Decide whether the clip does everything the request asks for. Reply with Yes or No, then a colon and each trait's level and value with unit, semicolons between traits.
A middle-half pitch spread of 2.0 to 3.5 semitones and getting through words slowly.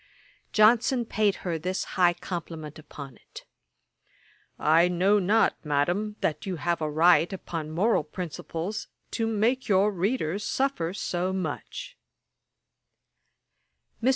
No: average, 4.5 semitones; slow, 120 wpm